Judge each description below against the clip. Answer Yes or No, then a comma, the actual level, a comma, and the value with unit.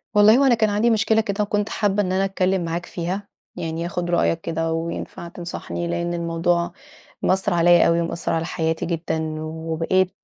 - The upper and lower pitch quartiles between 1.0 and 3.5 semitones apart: Yes, average, 2.8 semitones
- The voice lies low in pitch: No, medium, 175 Hz